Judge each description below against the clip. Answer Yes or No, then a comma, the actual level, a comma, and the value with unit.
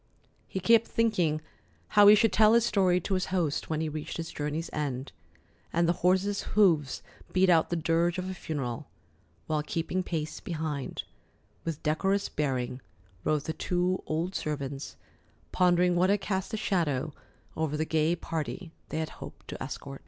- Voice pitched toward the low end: No, medium, 165 Hz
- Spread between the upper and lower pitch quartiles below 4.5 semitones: Yes, average, 3.5 semitones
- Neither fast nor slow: Yes, average, 165 wpm